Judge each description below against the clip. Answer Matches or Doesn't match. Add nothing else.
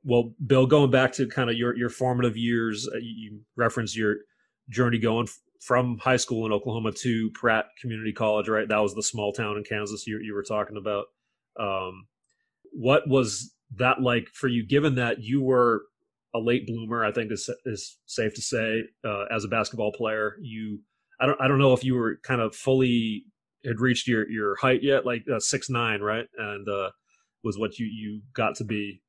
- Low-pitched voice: Matches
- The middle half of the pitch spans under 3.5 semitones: Matches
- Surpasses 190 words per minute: Matches